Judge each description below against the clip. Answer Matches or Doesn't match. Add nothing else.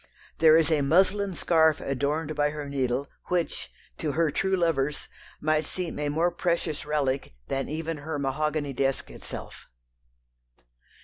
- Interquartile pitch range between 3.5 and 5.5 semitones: Doesn't match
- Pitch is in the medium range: Matches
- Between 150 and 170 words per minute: Doesn't match